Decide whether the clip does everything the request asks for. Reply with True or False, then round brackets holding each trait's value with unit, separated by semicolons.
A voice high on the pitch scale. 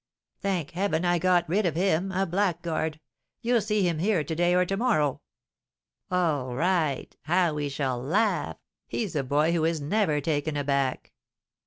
False (170 Hz)